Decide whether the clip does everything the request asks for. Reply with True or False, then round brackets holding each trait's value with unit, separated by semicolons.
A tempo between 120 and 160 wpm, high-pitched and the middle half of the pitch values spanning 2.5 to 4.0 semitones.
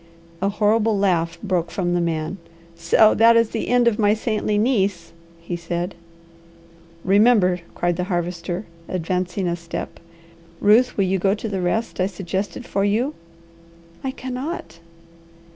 True (145 wpm; 195 Hz; 3.7 semitones)